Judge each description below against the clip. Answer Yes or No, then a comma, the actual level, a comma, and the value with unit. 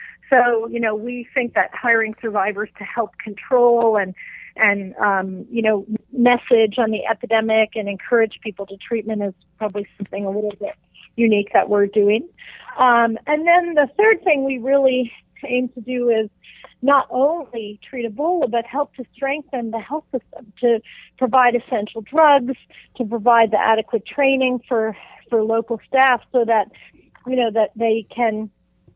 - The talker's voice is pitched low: No, high, 230 Hz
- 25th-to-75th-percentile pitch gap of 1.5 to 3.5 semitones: Yes, average, 2.9 semitones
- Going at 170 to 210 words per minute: No, average, 160 wpm